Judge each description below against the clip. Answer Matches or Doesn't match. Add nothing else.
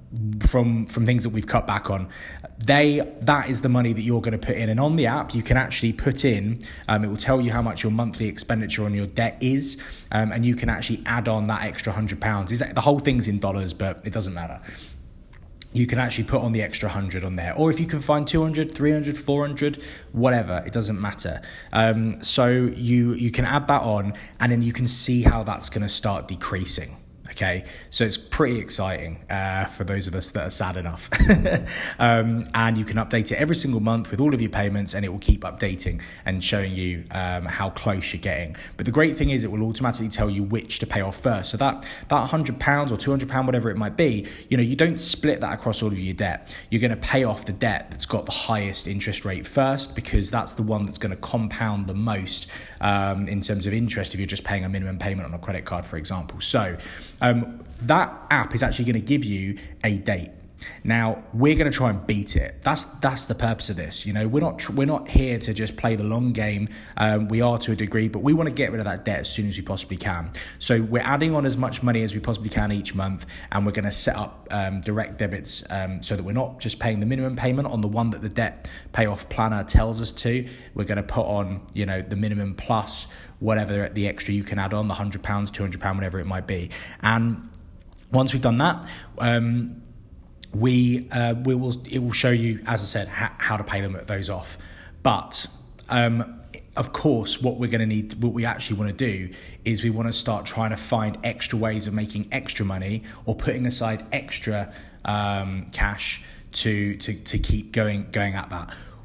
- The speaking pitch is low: Matches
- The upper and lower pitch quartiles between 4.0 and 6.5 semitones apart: Doesn't match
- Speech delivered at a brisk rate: Matches